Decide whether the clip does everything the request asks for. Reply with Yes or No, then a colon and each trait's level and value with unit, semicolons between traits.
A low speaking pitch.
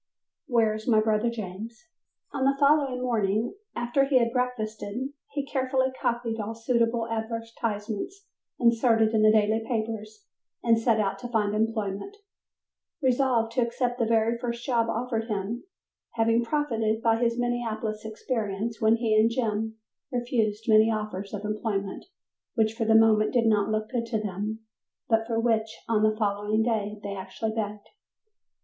No: high, 225 Hz